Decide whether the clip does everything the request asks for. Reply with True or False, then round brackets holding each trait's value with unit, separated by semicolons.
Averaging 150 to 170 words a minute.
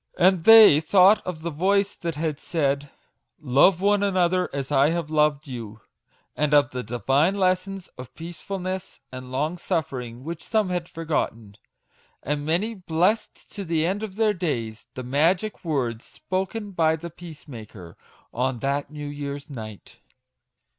True (155 wpm)